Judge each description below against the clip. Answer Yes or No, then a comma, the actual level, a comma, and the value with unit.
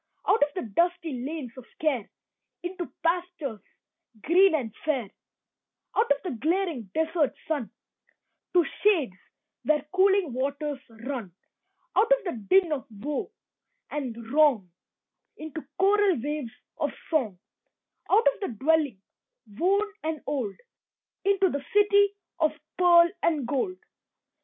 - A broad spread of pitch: Yes, wide, 6.0 semitones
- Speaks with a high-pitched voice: Yes, very high, 310 Hz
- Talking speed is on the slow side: Yes, slow, 125 wpm